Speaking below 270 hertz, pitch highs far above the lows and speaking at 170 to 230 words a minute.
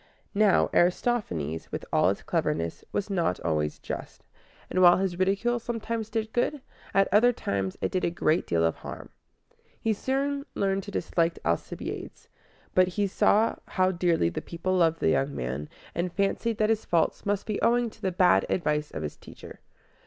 Yes: medium, 185 Hz; wide, 5.8 semitones; average, 175 wpm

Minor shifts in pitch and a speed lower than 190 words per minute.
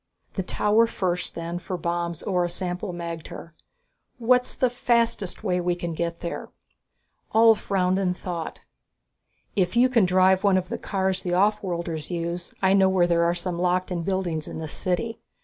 Yes: narrow, 2.2 semitones; average, 175 wpm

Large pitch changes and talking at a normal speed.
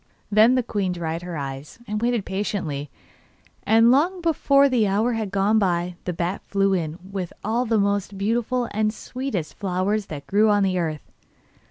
No: average, 4.0 semitones; average, 175 wpm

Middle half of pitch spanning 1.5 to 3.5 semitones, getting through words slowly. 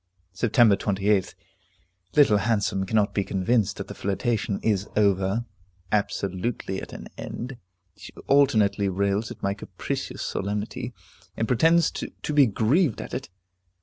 Yes: average, 3.1 semitones; slow, 130 wpm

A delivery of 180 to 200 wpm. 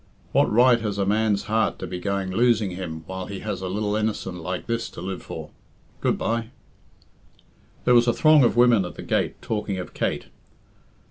Yes: average, 195 wpm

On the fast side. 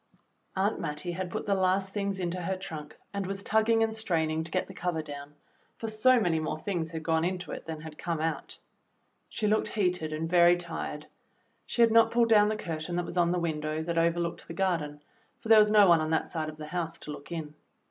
Yes: fast, 235 wpm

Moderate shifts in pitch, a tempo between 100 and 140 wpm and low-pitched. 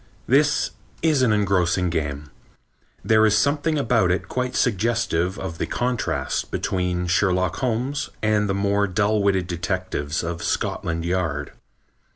Yes: average, 4.6 semitones; slow, 135 wpm; low, 100 Hz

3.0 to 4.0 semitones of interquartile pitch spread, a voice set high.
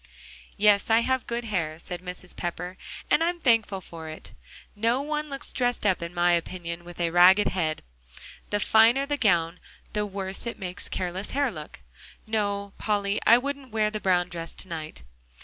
No: average, 4.6 semitones; high, 200 Hz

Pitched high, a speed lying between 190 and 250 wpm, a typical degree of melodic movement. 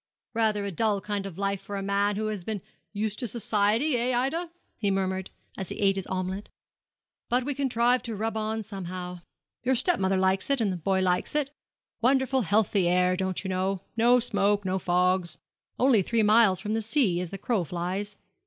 Yes: high, 205 Hz; average, 200 wpm; average, 3.4 semitones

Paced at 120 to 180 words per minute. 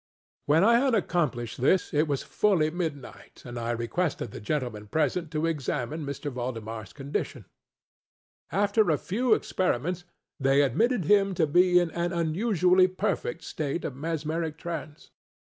Yes: average, 140 wpm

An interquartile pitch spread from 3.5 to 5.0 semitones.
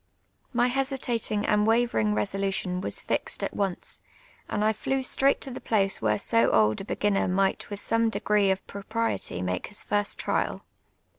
No: average, 3.1 semitones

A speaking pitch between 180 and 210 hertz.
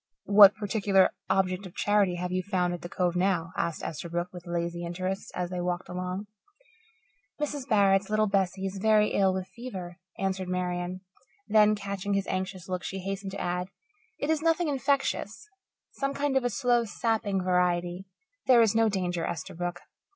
Yes: high, 190 Hz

